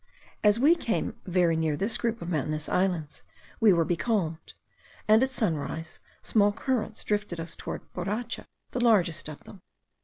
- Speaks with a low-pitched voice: No, high, 190 Hz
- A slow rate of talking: No, average, 155 wpm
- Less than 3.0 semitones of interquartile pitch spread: No, average, 5.2 semitones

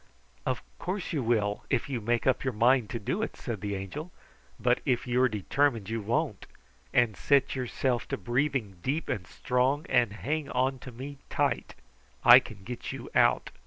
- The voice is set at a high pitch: No, low, 125 Hz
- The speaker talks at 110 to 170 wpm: No, average, 185 wpm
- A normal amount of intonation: Yes, average, 3.6 semitones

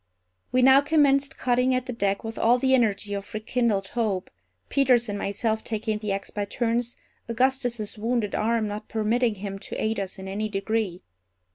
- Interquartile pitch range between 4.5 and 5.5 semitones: No, average, 3.3 semitones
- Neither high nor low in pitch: No, high, 225 Hz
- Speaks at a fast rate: No, average, 175 wpm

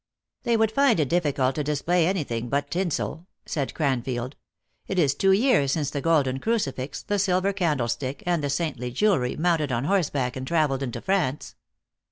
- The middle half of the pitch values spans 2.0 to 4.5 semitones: No, average, 5.3 semitones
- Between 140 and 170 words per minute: No, average, 185 wpm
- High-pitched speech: No, medium, 150 Hz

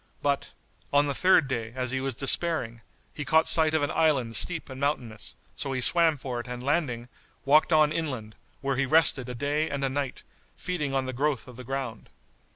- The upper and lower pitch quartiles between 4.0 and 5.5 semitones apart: No, average, 3.3 semitones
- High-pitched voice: No, low, 135 Hz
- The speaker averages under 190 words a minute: No, fast, 205 wpm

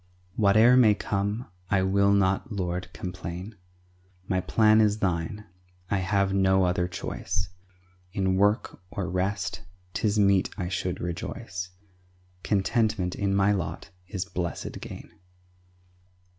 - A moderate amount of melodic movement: No, narrow, 2.1 semitones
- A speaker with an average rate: No, slow, 120 wpm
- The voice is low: Yes, very low, 95 Hz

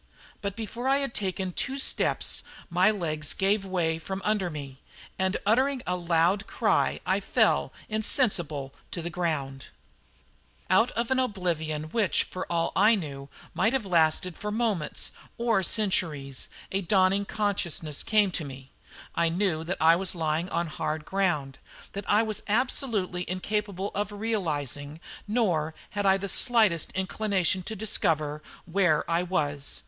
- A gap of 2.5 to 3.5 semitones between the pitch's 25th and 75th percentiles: No, average, 4.6 semitones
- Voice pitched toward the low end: No, medium, 185 Hz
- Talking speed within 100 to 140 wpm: No, average, 150 wpm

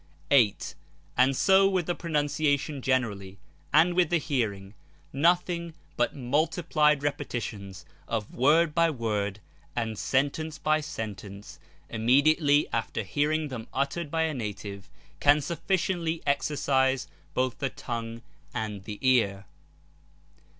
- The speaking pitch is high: No, medium, 140 Hz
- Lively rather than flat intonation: Yes, wide, 5.7 semitones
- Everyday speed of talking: No, slow, 120 wpm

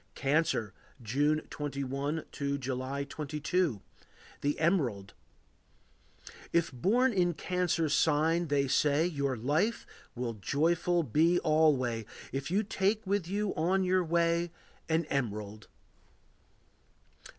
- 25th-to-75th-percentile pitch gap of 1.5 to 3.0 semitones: No, average, 4.1 semitones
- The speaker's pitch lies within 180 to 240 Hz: No, medium, 155 Hz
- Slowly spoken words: Yes, slow, 105 wpm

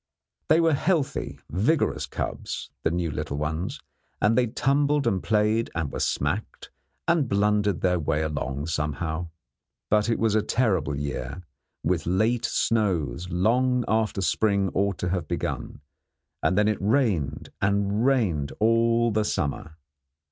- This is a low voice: Yes, low, 100 Hz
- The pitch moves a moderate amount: No, wide, 5.8 semitones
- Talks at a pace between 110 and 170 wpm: Yes, average, 140 wpm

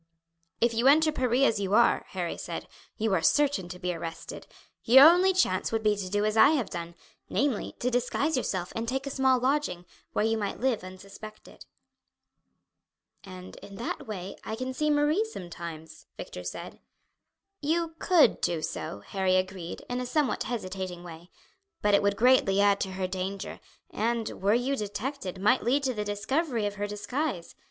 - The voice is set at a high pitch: Yes, high, 215 Hz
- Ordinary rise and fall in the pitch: No, wide, 5.8 semitones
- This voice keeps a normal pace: Yes, average, 180 wpm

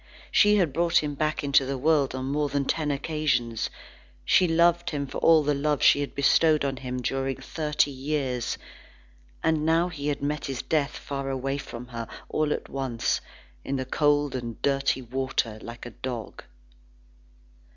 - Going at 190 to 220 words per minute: No, average, 170 wpm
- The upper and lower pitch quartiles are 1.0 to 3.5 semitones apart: Yes, narrow, 2.6 semitones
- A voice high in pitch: No, medium, 140 Hz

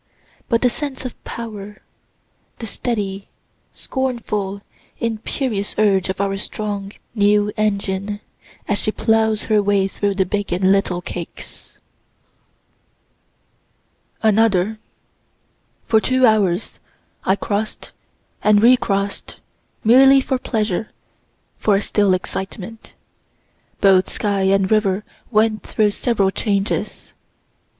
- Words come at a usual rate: No, slow, 105 wpm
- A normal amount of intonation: No, narrow, 2.1 semitones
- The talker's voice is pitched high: Yes, high, 205 Hz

